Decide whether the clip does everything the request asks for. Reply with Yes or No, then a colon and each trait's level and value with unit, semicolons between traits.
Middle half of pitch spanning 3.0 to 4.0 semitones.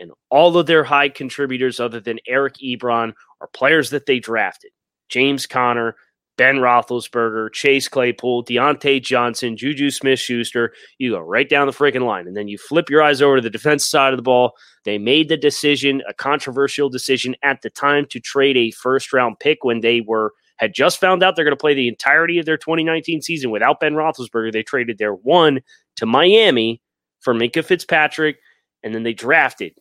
Yes: average, 3.6 semitones